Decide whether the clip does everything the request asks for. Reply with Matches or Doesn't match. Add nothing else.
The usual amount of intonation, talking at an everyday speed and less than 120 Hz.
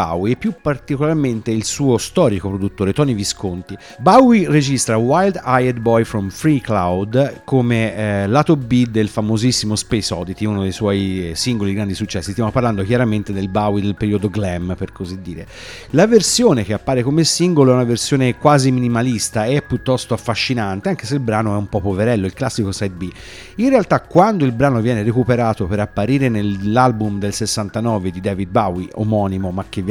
Doesn't match